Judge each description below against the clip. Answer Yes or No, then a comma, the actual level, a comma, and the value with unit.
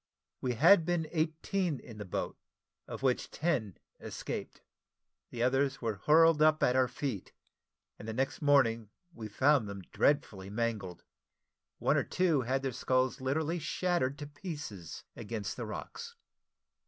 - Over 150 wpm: No, average, 145 wpm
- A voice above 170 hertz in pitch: No, low, 130 Hz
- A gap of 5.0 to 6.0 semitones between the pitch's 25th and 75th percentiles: Yes, wide, 5.5 semitones